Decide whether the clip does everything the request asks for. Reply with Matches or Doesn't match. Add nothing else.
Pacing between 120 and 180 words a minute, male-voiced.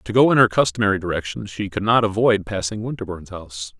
Doesn't match